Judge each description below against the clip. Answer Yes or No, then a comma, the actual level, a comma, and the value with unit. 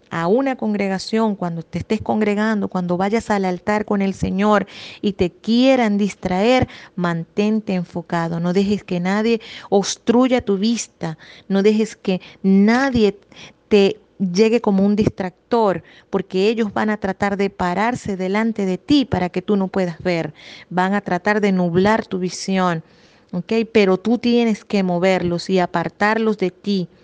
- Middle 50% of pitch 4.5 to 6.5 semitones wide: No, average, 3.0 semitones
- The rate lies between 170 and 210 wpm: No, average, 155 wpm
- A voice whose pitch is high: Yes, high, 200 Hz